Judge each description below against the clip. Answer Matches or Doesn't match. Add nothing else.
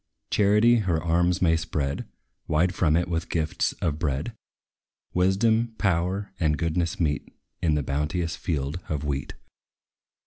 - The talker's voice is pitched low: Matches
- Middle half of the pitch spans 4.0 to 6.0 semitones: Doesn't match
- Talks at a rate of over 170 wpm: Doesn't match